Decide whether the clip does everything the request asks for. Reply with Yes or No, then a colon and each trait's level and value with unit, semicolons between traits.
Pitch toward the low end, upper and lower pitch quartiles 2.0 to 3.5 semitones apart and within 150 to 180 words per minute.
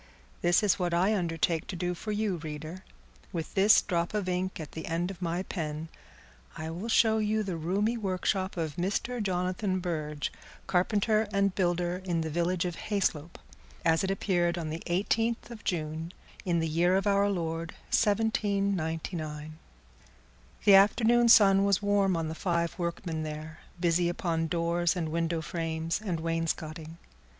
No: medium, 175 Hz; average, 3.2 semitones; average, 160 wpm